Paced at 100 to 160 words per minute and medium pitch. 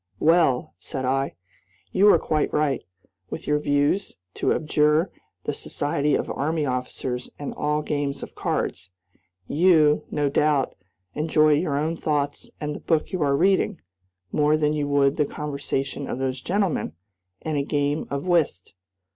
Yes: average, 155 wpm; medium, 150 Hz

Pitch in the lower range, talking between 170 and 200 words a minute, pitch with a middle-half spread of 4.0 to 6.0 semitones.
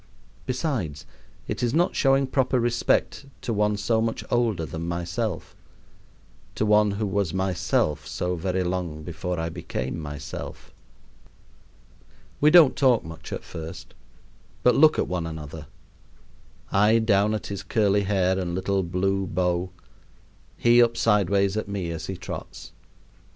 No: very low, 95 Hz; average, 140 wpm; average, 4.7 semitones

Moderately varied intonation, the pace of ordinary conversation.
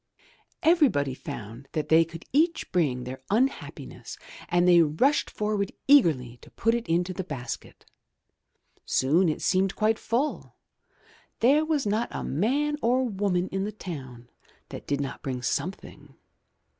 No: wide, 8.4 semitones; average, 145 wpm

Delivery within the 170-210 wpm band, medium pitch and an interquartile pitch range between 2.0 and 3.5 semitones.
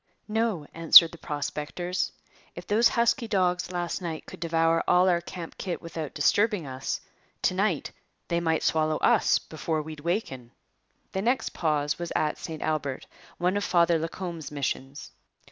No: average, 155 wpm; medium, 165 Hz; average, 2.8 semitones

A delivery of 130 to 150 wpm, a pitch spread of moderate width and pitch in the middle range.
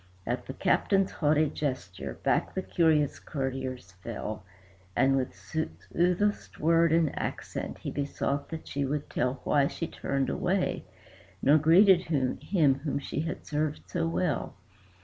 Yes: average, 140 wpm; average, 3.7 semitones; medium, 145 Hz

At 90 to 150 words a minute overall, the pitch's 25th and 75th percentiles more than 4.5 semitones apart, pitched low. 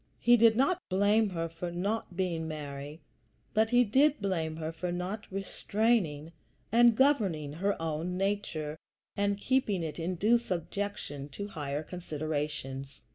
No: average, 140 wpm; average, 5.2 semitones; medium, 180 Hz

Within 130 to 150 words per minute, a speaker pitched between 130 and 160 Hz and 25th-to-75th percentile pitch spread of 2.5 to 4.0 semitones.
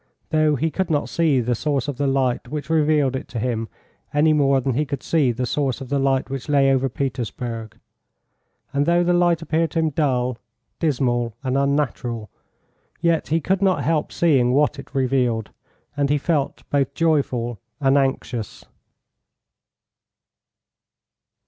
No: average, 160 wpm; medium, 140 Hz; average, 3.3 semitones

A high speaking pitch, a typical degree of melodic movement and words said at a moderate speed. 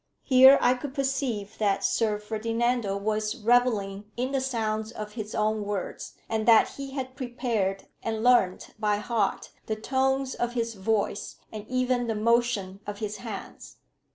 Yes: high, 225 Hz; average, 3.0 semitones; average, 155 wpm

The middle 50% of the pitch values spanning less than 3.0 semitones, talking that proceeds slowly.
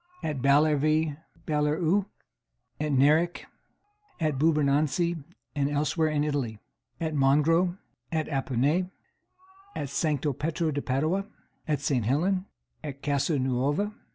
Yes: narrow, 2.6 semitones; slow, 110 wpm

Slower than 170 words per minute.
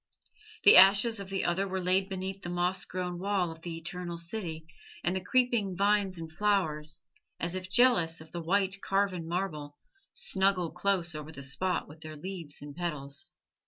No: average, 175 wpm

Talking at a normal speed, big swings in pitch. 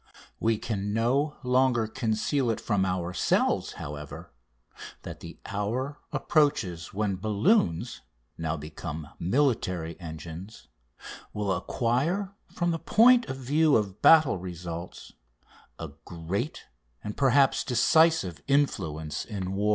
No: slow, 110 wpm; wide, 7.6 semitones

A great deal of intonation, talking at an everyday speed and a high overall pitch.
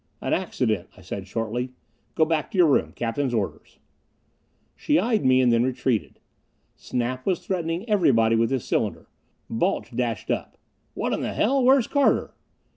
No: wide, 7.9 semitones; average, 160 wpm; low, 130 Hz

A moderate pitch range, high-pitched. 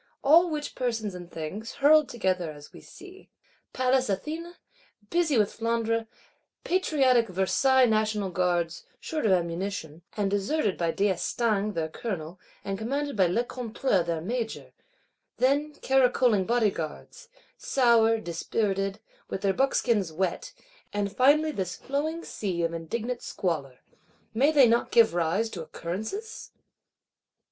No: wide, 6.2 semitones; high, 220 Hz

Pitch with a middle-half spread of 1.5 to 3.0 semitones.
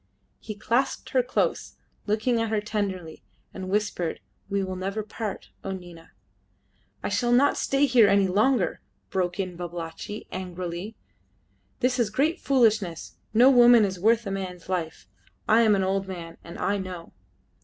No: average, 3.9 semitones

